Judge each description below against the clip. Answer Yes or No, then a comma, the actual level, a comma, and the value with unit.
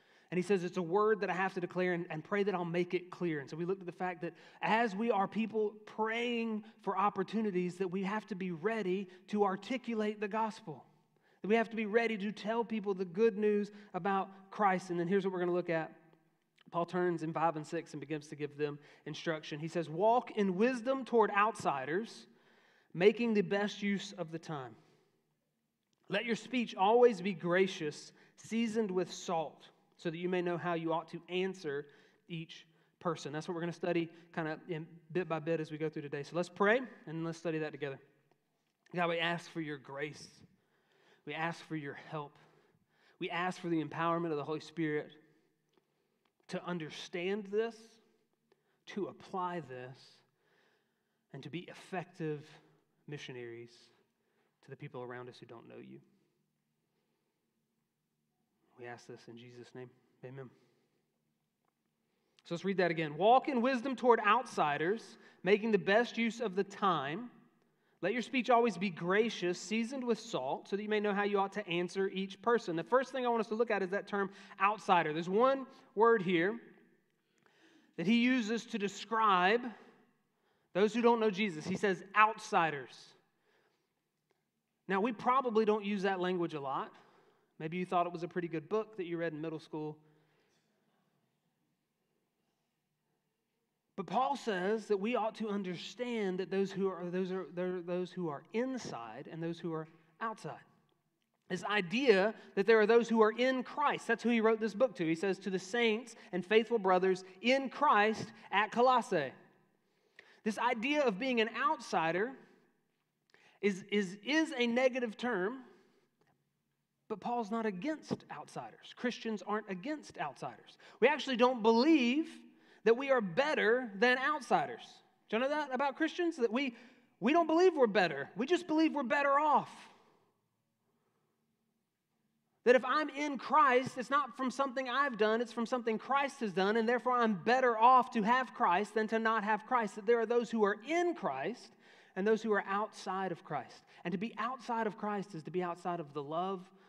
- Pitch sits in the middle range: No, high, 200 Hz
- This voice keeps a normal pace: Yes, average, 180 wpm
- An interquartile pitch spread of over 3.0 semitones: Yes, average, 5.2 semitones